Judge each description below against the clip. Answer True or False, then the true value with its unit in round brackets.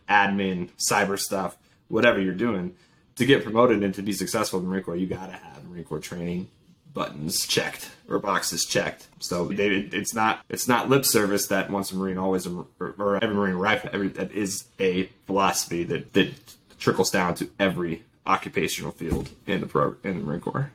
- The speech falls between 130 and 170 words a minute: False (190 wpm)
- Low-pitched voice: True (95 Hz)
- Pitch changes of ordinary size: False (2.1 semitones)